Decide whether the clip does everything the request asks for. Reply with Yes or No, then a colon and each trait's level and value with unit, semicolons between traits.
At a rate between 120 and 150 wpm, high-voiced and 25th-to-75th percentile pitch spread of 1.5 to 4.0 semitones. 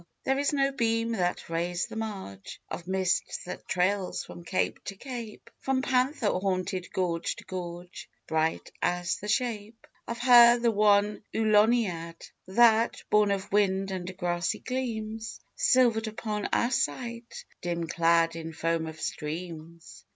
No: average, 145 wpm; high, 200 Hz; average, 4.8 semitones